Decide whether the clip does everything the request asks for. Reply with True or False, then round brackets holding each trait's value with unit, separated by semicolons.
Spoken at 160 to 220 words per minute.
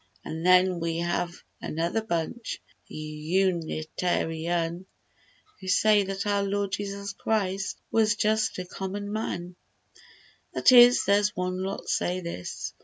False (135 wpm)